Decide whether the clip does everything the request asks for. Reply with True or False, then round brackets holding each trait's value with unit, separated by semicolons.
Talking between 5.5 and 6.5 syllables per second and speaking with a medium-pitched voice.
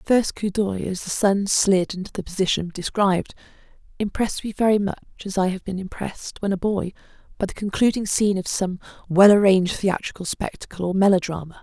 False (5.8 syllables/s; 195 Hz)